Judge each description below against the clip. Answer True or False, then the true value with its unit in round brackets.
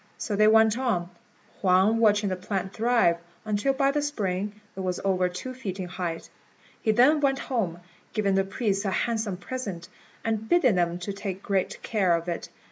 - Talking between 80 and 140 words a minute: False (180 wpm)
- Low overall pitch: False (200 Hz)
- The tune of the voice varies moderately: True (3.7 semitones)